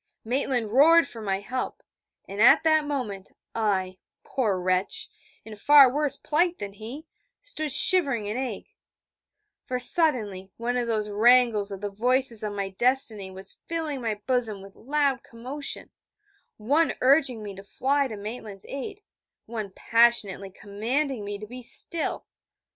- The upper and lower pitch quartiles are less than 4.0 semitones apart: No, average, 5.1 semitones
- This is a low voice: No, high, 235 Hz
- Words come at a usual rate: Yes, average, 145 wpm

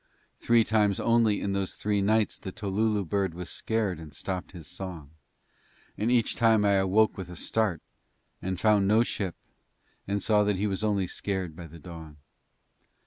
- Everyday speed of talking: Yes, average, 175 wpm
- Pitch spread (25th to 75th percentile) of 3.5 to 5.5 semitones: No, average, 2.9 semitones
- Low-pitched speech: Yes, low, 100 Hz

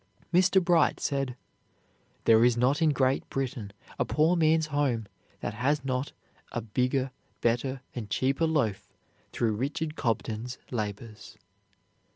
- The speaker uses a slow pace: Yes, slow, 130 wpm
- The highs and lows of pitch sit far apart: No, average, 4.2 semitones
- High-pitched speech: No, low, 130 Hz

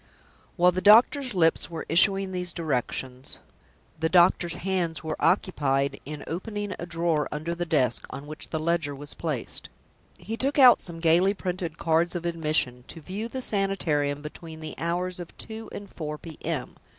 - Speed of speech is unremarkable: Yes, average, 165 wpm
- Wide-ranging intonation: No, average, 3.4 semitones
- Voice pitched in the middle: Yes, medium, 170 Hz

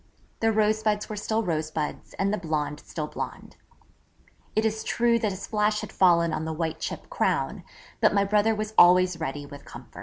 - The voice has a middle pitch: No, high, 195 Hz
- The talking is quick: No, average, 185 wpm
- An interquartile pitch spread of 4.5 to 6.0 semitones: Yes, average, 5.0 semitones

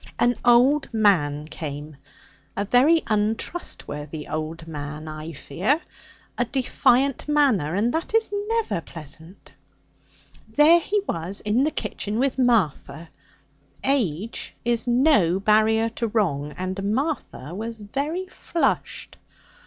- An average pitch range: No, wide, 8.4 semitones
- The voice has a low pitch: No, high, 215 Hz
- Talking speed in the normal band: No, slow, 115 wpm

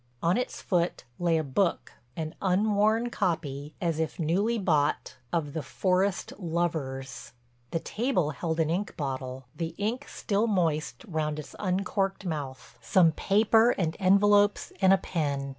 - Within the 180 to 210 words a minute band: No, average, 145 wpm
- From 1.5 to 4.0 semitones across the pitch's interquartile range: No, average, 4.6 semitones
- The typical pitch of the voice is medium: Yes, medium, 170 Hz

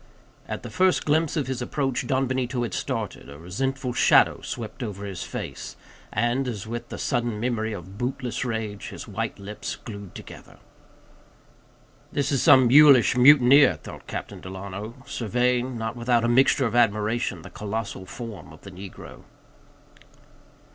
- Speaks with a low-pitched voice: Yes, low, 120 Hz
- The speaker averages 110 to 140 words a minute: No, average, 155 wpm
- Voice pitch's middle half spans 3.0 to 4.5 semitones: Yes, average, 3.9 semitones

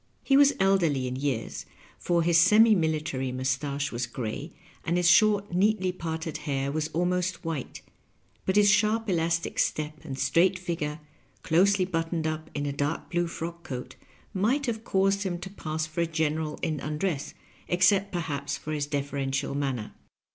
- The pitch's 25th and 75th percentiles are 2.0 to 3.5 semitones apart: No, average, 4.4 semitones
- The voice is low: No, medium, 165 Hz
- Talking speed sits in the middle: Yes, average, 160 wpm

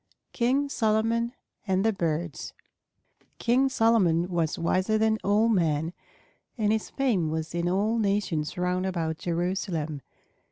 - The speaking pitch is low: No, high, 190 Hz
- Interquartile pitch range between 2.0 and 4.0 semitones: No, average, 4.8 semitones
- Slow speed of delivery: Yes, slow, 125 wpm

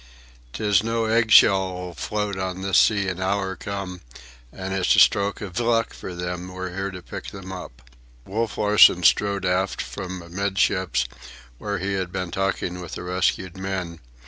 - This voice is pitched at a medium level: No, very low, 95 Hz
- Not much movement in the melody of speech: Yes, narrow, 1.7 semitones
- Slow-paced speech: No, average, 170 wpm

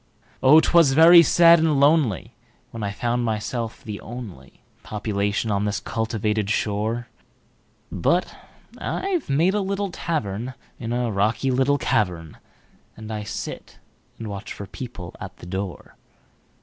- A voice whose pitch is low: Yes, low, 115 Hz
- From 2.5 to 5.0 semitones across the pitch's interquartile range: No, wide, 5.6 semitones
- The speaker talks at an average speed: No, slow, 120 wpm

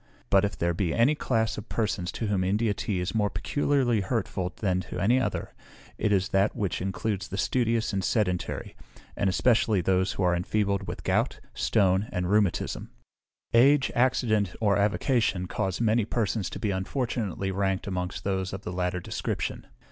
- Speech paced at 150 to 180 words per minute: Yes, average, 170 wpm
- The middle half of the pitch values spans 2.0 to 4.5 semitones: Yes, average, 3.2 semitones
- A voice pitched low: Yes, low, 100 Hz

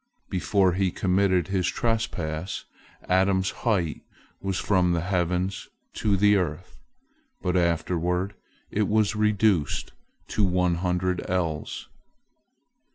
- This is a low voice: Yes, very low, 95 Hz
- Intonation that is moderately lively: No, narrow, 2.0 semitones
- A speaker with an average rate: No, slow, 105 wpm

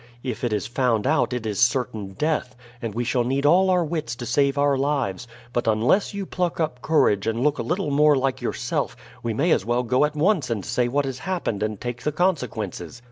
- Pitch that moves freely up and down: No, average, 4.5 semitones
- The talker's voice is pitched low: Yes, low, 130 Hz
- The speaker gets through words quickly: Yes, fast, 225 wpm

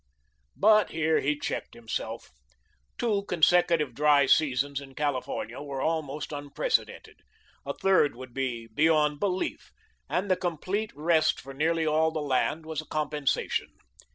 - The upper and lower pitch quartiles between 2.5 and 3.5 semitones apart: Yes, average, 2.8 semitones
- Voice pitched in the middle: Yes, medium, 150 Hz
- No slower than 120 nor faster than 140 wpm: Yes, slow, 135 wpm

